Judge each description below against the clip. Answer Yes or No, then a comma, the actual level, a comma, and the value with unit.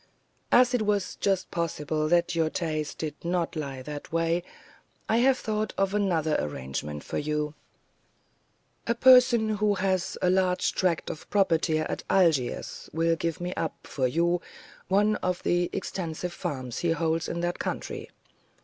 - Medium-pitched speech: Yes, medium, 170 Hz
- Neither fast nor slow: Yes, average, 155 wpm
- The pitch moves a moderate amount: Yes, average, 3.7 semitones